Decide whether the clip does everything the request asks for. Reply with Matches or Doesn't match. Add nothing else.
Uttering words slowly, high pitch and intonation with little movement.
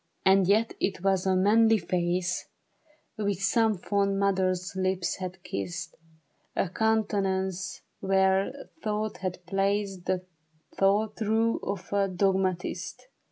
Matches